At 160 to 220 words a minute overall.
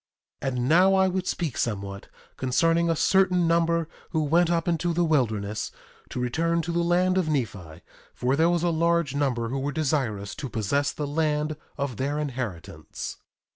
Yes: average, 175 wpm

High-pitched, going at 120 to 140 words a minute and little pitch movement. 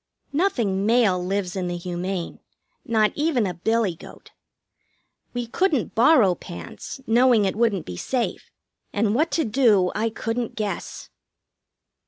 No: high, 215 Hz; slow, 135 wpm; average, 4.5 semitones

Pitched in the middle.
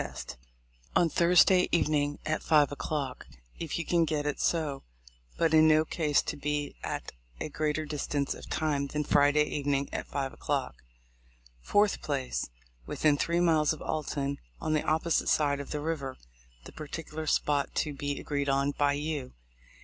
Yes: medium, 150 Hz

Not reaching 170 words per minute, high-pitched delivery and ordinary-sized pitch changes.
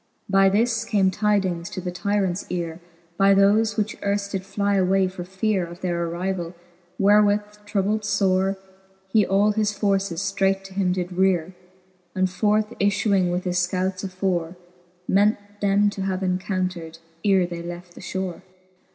No: average, 155 wpm; high, 195 Hz; narrow, 1.9 semitones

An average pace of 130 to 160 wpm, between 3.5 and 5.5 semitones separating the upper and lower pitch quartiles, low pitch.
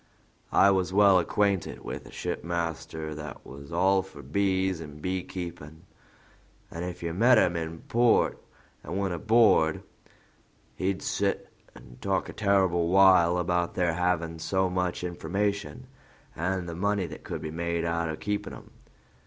No: average, 150 wpm; narrow, 2.6 semitones; very low, 90 Hz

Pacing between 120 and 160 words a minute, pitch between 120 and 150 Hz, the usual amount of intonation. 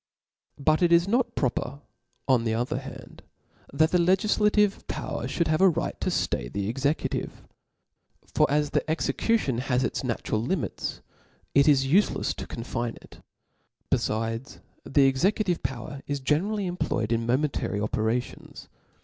No: average, 145 wpm; medium, 140 Hz; wide, 6.2 semitones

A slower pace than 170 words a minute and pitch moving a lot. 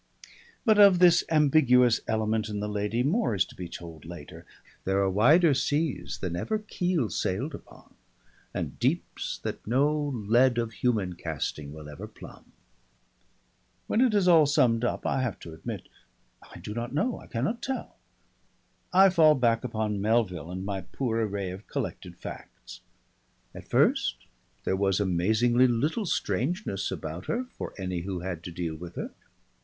Yes: average, 160 wpm; wide, 7.8 semitones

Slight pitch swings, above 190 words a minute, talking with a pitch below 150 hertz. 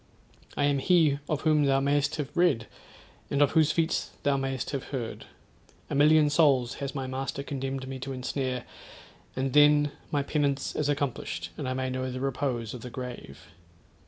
No: narrow, 2.1 semitones; average, 180 wpm; low, 135 Hz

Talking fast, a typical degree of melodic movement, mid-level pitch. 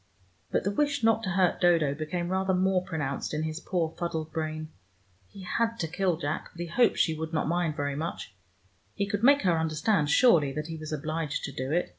Yes: fast, 215 wpm; average, 3.3 semitones; medium, 165 Hz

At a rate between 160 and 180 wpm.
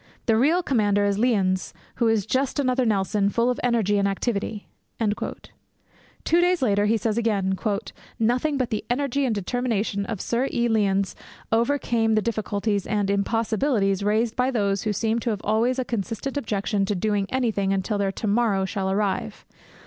Yes: average, 170 wpm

